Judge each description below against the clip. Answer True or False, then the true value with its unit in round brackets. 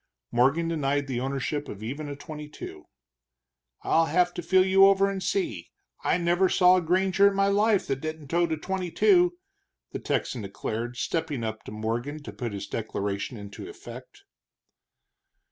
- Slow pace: False (170 wpm)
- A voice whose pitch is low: False (155 Hz)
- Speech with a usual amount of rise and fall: False (7.1 semitones)